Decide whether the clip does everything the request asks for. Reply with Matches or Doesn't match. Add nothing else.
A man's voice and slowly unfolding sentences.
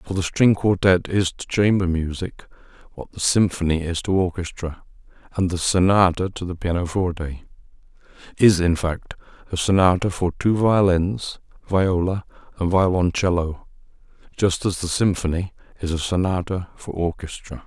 Matches